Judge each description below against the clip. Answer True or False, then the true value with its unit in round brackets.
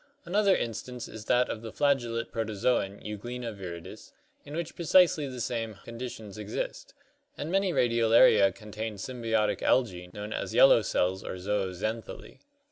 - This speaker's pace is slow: False (155 wpm)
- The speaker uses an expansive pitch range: False (3.4 semitones)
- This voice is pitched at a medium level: False (115 Hz)